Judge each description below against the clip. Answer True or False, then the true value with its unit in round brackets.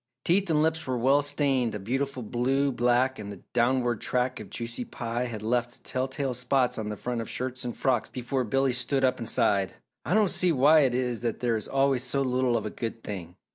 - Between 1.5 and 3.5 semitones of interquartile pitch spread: True (2.4 semitones)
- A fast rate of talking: True (220 wpm)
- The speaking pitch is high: False (125 Hz)